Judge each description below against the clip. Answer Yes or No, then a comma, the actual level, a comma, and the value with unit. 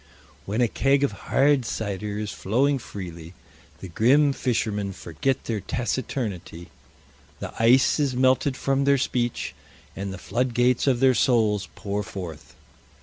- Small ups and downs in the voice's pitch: No, average, 4.8 semitones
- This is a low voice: Yes, low, 120 Hz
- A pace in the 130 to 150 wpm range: Yes, average, 140 wpm